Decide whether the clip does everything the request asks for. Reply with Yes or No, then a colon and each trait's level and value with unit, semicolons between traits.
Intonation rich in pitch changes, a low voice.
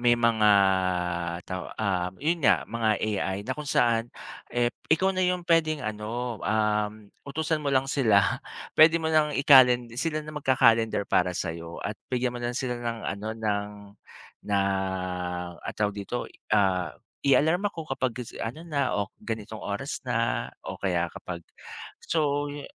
Yes: wide, 5.8 semitones; low, 120 Hz